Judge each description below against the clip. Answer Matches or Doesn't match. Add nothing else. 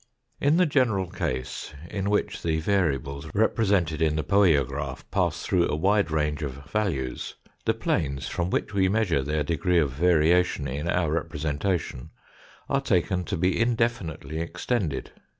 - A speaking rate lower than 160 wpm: Matches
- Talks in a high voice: Doesn't match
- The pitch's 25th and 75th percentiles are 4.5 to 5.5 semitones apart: Matches